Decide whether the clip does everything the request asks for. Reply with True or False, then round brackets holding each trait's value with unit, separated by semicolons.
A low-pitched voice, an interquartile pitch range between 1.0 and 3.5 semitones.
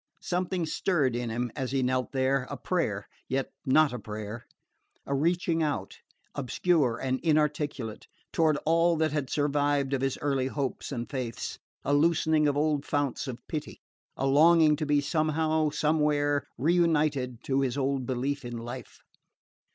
False (145 Hz; 3.0 semitones)